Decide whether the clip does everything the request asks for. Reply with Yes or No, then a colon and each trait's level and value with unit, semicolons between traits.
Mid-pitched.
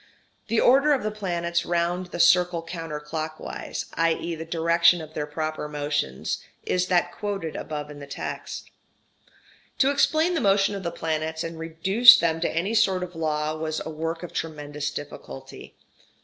Yes: medium, 165 Hz